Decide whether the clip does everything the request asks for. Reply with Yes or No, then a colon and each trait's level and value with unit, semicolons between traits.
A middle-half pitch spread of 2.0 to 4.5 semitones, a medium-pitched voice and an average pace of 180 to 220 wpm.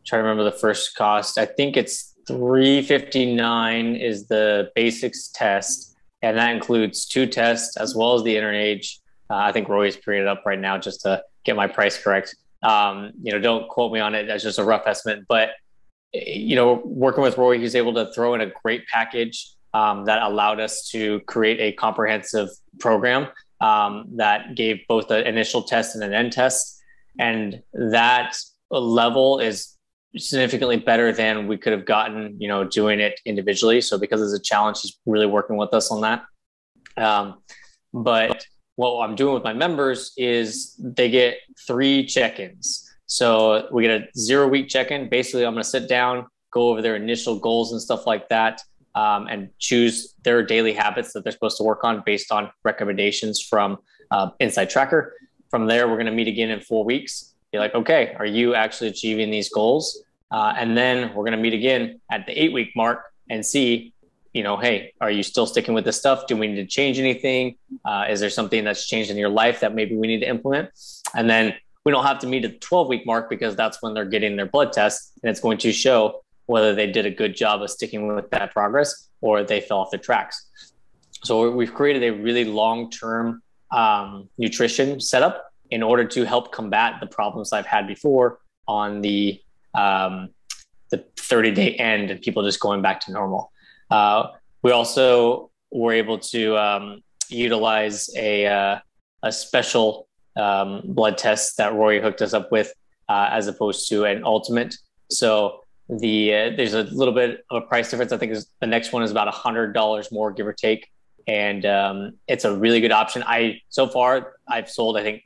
No: narrow, 2.6 semitones; low, 115 Hz; average, 200 wpm